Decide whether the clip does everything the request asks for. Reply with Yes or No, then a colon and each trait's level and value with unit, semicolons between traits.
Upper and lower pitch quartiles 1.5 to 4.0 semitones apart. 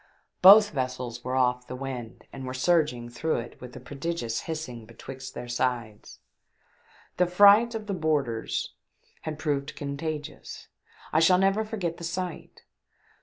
No: wide, 5.6 semitones